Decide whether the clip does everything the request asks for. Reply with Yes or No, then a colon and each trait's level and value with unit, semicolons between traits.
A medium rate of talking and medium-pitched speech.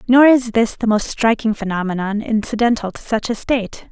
No: average, 185 wpm; high, 220 Hz